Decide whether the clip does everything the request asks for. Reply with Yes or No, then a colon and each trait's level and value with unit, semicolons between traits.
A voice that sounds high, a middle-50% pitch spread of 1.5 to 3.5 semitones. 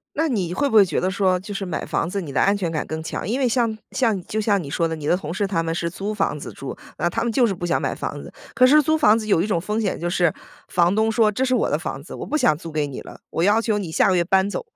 No: high, 195 Hz; average, 4.7 semitones